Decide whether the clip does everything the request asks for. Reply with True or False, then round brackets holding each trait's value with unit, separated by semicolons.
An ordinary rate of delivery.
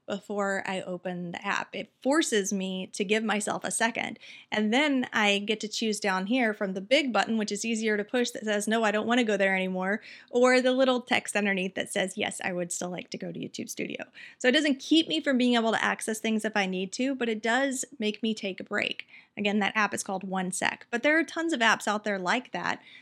False (250 wpm)